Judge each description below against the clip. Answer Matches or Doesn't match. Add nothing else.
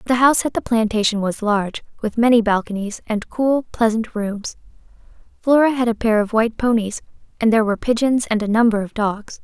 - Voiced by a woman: Matches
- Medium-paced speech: Matches